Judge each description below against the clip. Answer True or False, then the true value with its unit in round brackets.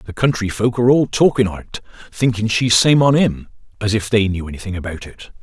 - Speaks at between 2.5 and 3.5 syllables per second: False (5.5 syllables/s)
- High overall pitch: False (110 Hz)